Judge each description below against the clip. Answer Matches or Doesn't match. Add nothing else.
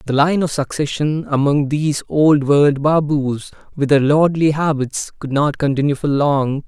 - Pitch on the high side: Doesn't match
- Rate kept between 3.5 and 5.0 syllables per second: Matches